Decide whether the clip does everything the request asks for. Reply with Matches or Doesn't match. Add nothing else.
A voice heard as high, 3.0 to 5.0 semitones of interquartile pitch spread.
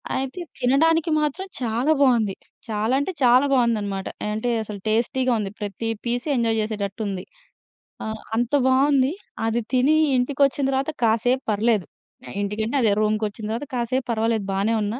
Matches